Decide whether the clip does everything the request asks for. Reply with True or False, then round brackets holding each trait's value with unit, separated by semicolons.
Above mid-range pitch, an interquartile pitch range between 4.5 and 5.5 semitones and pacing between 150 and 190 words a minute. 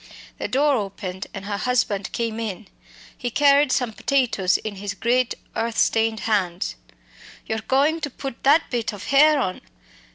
True (230 Hz; 5.0 semitones; 160 wpm)